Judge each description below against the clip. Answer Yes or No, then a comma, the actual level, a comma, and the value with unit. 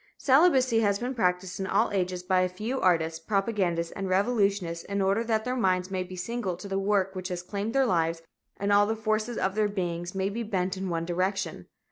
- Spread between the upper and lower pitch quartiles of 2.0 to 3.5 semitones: Yes, average, 3.1 semitones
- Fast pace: Yes, fast, 215 wpm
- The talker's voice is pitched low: No, high, 195 Hz